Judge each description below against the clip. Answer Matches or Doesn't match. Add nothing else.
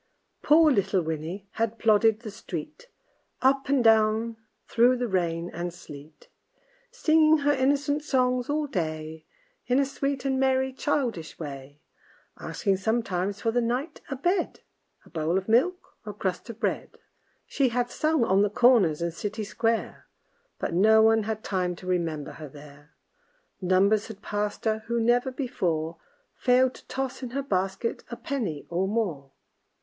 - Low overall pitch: Doesn't match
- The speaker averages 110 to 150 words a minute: Doesn't match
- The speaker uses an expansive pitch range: Matches